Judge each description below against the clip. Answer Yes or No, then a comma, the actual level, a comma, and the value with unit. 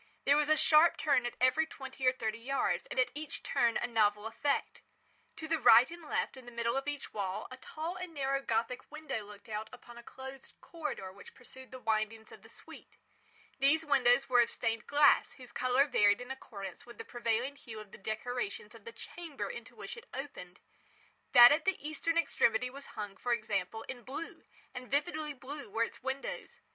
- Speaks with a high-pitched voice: Yes, very high, 255 Hz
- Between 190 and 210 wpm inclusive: Yes, average, 200 wpm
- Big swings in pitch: No, average, 4.1 semitones